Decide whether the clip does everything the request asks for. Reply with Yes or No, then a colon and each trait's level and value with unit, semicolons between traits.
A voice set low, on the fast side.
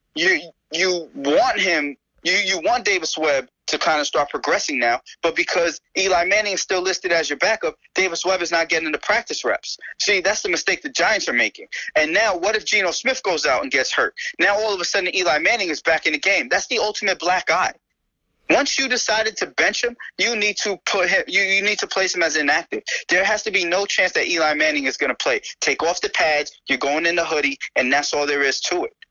No: high, 190 Hz; fast, 240 wpm